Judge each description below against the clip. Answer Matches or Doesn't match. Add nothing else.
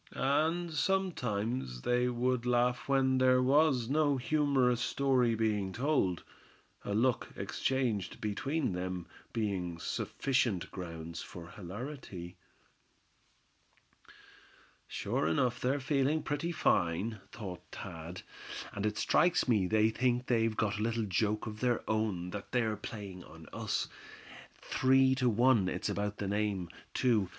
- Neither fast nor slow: Doesn't match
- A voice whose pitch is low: Matches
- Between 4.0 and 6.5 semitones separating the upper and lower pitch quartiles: Matches